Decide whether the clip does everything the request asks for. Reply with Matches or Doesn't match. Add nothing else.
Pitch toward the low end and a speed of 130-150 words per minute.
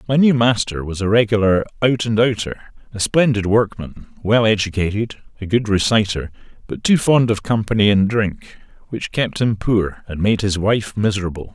Doesn't match